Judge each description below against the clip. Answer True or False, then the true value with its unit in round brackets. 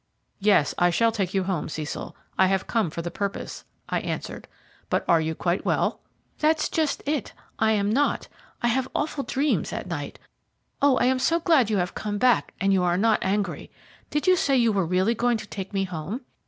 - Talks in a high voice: True (210 Hz)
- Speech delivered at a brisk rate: True (210 wpm)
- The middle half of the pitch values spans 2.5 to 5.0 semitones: False (5.5 semitones)